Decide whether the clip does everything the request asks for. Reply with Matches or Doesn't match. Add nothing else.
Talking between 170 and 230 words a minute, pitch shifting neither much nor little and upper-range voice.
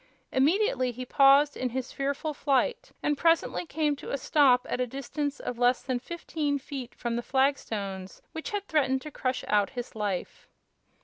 Matches